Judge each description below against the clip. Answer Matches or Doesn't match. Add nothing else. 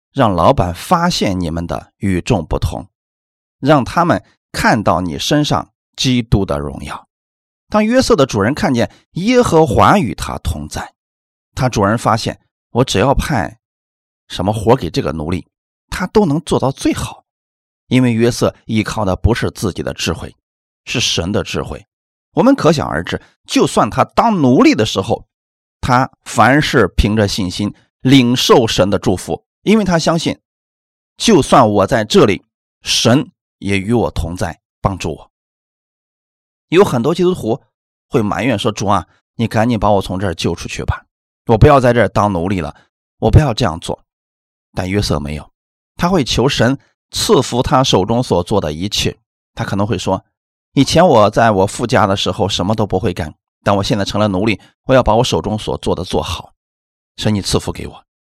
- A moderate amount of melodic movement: Doesn't match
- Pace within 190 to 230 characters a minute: Doesn't match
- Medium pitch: Doesn't match